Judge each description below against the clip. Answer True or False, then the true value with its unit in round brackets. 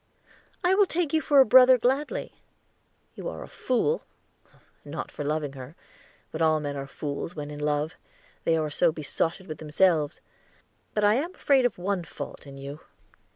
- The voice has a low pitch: False (165 Hz)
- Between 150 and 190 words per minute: True (175 wpm)